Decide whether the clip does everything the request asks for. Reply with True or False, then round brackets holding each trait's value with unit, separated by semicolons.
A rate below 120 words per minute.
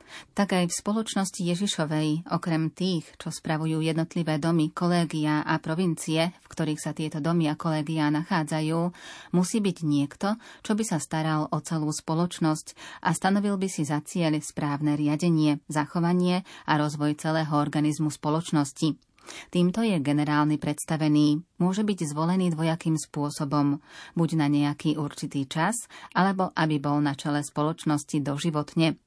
False (140 wpm)